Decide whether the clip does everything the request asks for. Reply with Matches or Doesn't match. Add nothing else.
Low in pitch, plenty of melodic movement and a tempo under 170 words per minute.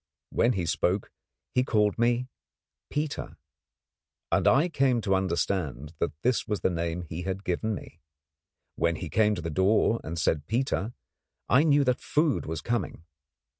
Matches